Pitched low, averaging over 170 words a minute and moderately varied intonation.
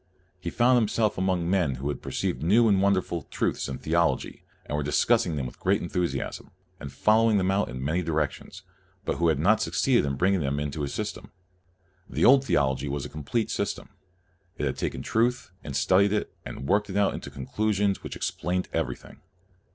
No: very low, 90 Hz; average, 190 wpm; wide, 6.3 semitones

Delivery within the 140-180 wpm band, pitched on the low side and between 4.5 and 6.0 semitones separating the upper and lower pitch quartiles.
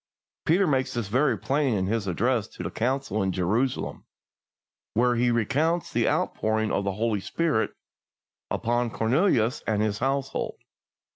No: average, 145 wpm; low, 120 Hz; average, 3.8 semitones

